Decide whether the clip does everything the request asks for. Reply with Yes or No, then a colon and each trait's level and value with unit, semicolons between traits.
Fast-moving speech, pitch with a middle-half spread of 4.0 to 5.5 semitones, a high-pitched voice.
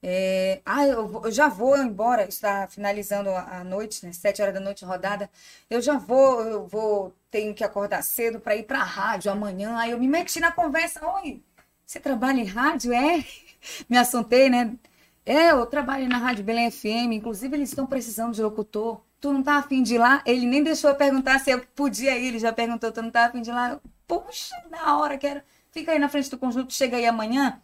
Yes: fast, 215 wpm; average, 4.5 semitones; high, 245 Hz